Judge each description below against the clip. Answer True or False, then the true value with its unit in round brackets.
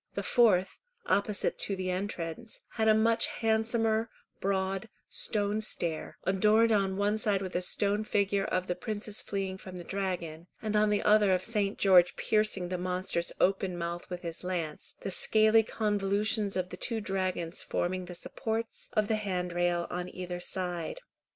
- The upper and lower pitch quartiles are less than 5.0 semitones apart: True (2.9 semitones)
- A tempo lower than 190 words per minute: True (165 wpm)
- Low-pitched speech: False (195 Hz)